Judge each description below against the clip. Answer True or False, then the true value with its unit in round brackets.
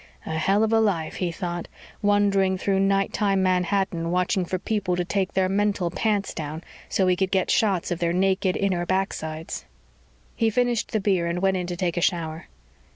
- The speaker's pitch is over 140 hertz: True (190 Hz)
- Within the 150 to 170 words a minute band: False (190 wpm)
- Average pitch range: False (2.2 semitones)